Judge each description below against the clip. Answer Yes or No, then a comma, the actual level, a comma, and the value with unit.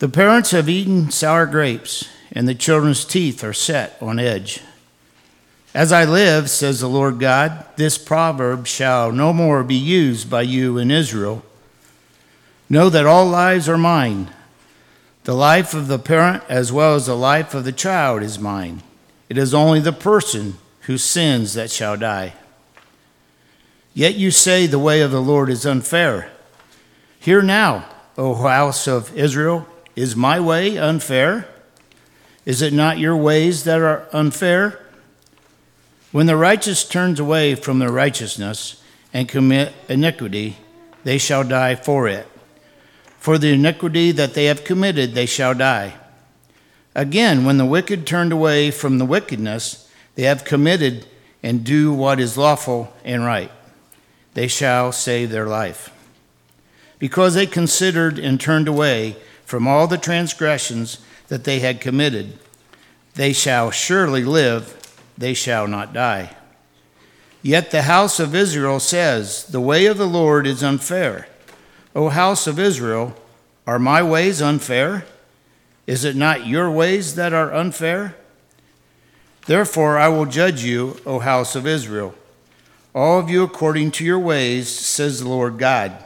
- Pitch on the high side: No, medium, 140 Hz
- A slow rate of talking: No, average, 150 wpm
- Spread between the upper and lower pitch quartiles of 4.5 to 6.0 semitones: Yes, wide, 5.4 semitones